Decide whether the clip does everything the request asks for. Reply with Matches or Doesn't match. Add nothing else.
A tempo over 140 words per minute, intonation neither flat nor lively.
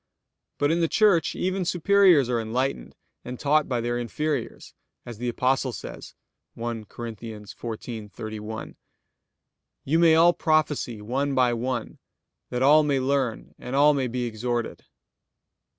Doesn't match